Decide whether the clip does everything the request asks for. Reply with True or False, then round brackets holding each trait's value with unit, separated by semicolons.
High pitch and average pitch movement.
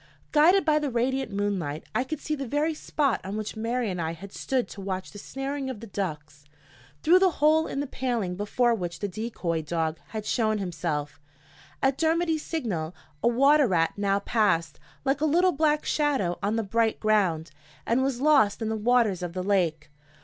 False (220 Hz; 7.1 semitones)